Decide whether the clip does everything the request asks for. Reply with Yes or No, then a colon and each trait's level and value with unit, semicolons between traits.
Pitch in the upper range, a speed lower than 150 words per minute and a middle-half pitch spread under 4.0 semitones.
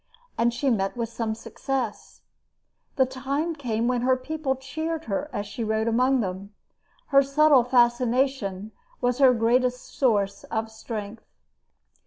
Yes: high, 245 Hz; average, 140 wpm; average, 3.3 semitones